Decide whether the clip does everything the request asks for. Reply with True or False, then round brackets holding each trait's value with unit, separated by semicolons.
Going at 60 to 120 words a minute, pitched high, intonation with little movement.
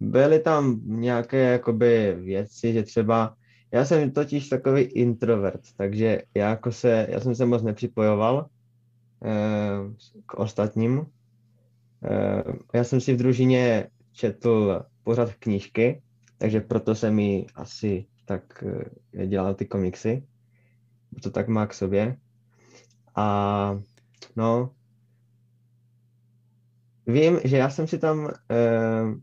False (115 wpm; 120 Hz; 2.0 semitones)